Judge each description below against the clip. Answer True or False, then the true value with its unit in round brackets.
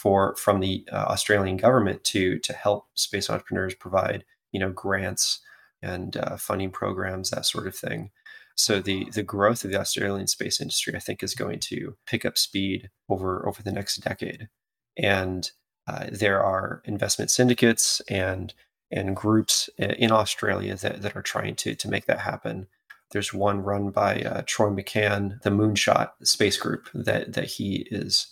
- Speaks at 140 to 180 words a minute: True (170 wpm)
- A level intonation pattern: True (1.5 semitones)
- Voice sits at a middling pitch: False (100 Hz)